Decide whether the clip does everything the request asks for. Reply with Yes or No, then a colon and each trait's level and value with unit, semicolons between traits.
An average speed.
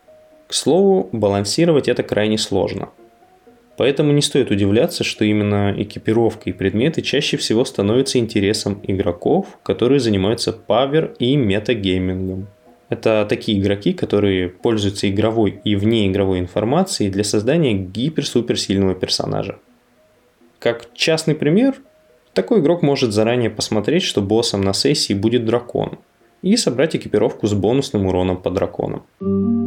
Yes: average, 125 wpm